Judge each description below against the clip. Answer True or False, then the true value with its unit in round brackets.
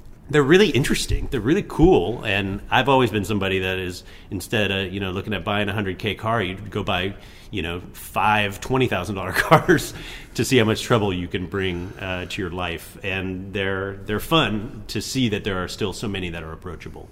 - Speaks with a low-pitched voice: True (100 Hz)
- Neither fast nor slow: False (210 wpm)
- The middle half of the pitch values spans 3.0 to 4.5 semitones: False (2.4 semitones)